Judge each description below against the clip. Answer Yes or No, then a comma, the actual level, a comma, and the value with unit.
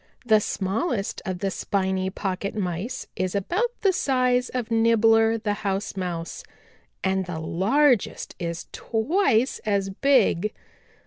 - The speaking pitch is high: Yes, high, 210 Hz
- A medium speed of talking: No, slow, 125 wpm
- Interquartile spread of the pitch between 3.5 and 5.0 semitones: Yes, average, 4.4 semitones